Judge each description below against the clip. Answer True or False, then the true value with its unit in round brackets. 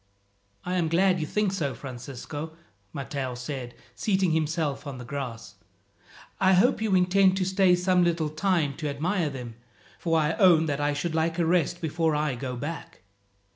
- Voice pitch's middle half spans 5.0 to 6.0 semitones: False (4.3 semitones)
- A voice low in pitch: False (160 Hz)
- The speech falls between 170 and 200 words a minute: True (175 wpm)